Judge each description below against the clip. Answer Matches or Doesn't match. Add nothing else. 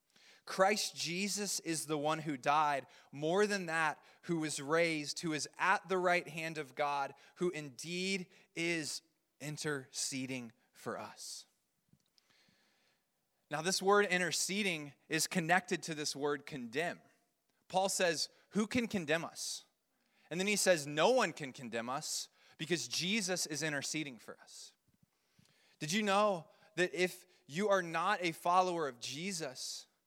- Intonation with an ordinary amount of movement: Matches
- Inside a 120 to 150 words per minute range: Matches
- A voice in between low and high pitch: Matches